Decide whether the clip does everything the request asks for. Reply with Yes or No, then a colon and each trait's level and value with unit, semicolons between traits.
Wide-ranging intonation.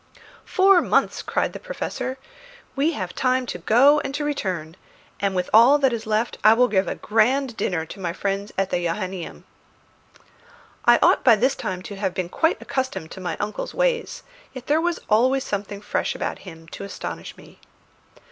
Yes: wide, 6.2 semitones